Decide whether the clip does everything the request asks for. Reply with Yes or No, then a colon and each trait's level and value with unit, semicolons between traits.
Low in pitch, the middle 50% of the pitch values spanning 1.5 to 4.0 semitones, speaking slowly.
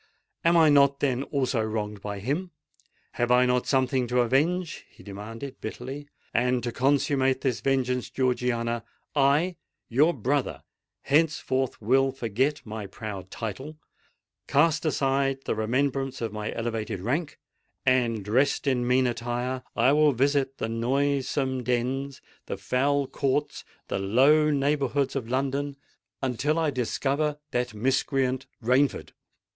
Yes: low, 130 Hz; average, 2.9 semitones; slow, 120 wpm